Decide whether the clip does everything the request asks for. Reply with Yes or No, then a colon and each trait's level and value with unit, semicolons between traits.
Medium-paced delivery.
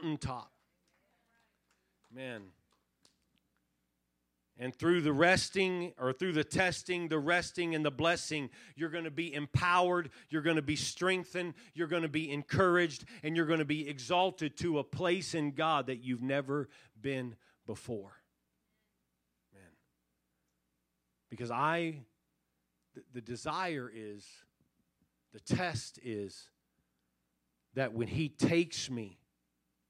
No: slow, 120 wpm